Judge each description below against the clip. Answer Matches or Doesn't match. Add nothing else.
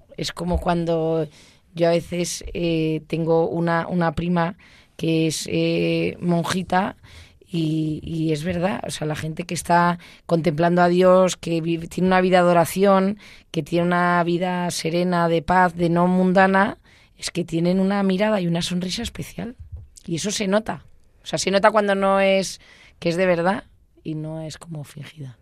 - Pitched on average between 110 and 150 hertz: Doesn't match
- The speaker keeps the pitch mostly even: Matches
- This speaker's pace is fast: Doesn't match